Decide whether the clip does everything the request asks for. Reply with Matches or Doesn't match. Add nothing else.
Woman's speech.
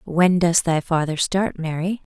Matches